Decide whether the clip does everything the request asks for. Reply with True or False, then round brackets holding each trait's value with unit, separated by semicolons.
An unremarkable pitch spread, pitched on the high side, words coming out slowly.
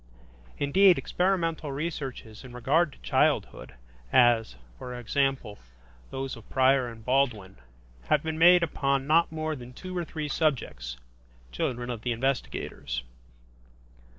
False (4.6 semitones; 135 Hz; 125 wpm)